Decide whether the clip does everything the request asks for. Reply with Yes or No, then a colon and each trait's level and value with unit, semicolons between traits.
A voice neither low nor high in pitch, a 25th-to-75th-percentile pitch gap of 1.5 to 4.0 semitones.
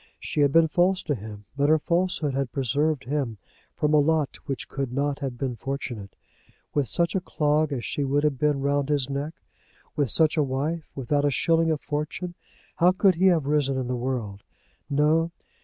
Yes: medium, 145 Hz; average, 2.7 semitones